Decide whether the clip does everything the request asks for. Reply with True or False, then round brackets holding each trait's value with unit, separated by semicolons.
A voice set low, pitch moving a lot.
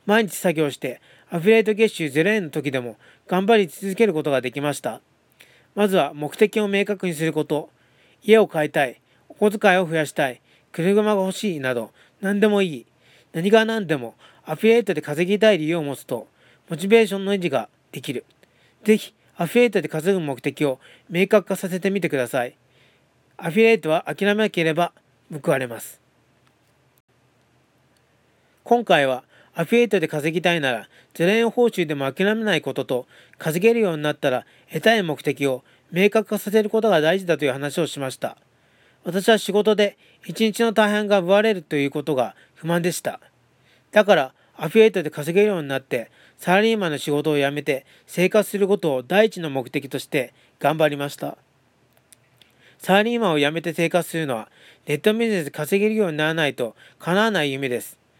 False (175 Hz; 5.9 semitones)